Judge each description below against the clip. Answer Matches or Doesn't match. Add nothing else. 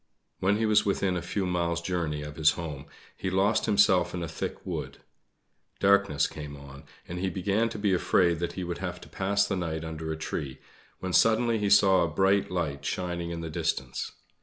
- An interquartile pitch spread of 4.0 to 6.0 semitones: Doesn't match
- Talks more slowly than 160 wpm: Doesn't match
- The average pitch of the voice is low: Matches